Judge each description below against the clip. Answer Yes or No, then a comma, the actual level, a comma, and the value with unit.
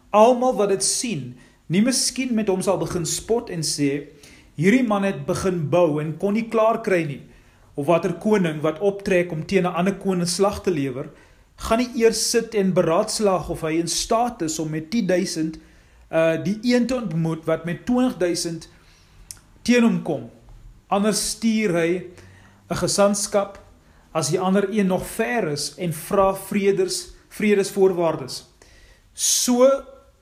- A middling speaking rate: Yes, average, 155 wpm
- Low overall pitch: No, medium, 180 Hz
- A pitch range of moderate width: Yes, average, 4.7 semitones